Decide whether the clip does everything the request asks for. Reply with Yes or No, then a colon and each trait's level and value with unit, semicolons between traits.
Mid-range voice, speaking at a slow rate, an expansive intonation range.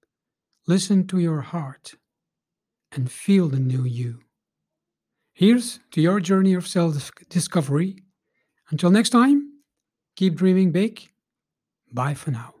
No: medium, 180 Hz; slow, 120 wpm; average, 4.8 semitones